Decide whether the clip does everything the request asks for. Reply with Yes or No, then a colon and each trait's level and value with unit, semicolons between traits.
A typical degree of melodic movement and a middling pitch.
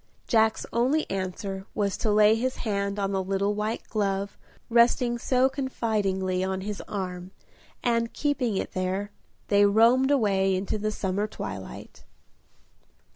No: average, 3.2 semitones; high, 205 Hz